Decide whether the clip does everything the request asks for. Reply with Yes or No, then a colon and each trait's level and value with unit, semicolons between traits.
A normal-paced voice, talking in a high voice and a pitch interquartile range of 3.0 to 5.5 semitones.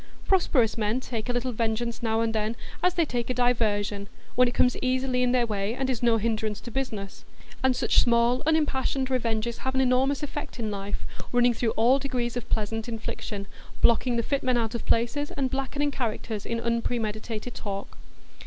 No: average, 190 wpm; high, 240 Hz; narrow, 2.5 semitones